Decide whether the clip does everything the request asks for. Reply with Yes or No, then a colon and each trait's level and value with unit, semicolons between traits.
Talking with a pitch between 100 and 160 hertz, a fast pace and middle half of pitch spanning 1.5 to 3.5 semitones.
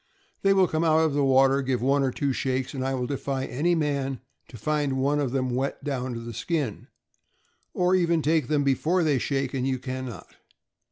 Yes: low, 135 Hz; fast, 215 wpm; average, 2.7 semitones